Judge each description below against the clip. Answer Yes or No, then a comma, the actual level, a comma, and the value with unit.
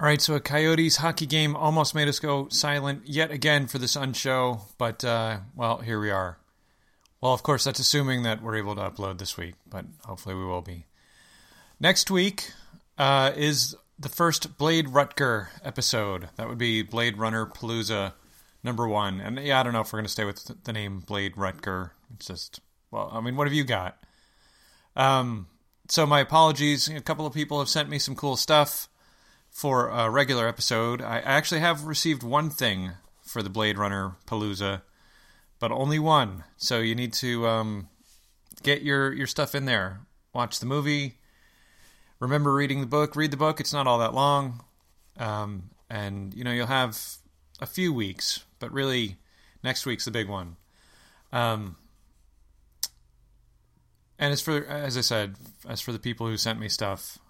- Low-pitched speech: Yes, low, 120 Hz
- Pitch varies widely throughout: Yes, wide, 6.0 semitones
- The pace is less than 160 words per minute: No, average, 180 wpm